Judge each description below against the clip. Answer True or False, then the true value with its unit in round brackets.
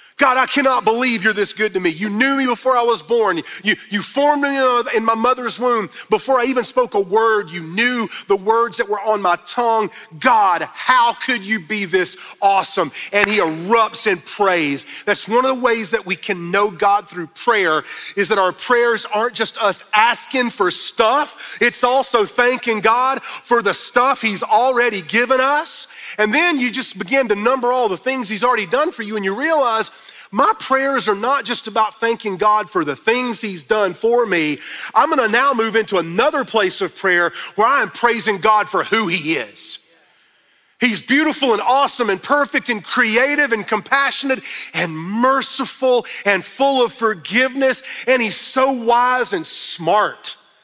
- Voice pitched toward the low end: False (230 Hz)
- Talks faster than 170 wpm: True (185 wpm)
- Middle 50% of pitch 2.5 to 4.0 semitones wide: True (3.7 semitones)